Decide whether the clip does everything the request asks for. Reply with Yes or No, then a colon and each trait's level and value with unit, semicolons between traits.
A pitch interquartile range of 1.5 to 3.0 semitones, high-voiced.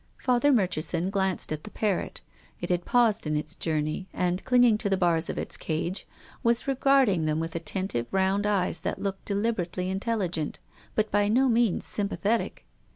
No: average, 4.3 semitones; high, 195 Hz